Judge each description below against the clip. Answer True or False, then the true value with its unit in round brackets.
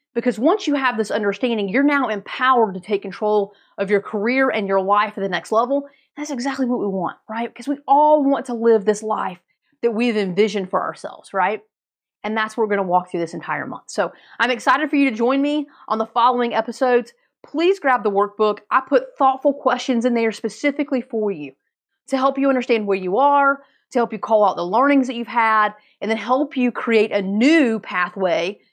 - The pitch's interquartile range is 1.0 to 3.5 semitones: False (4.4 semitones)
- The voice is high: True (235 Hz)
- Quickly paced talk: True (215 wpm)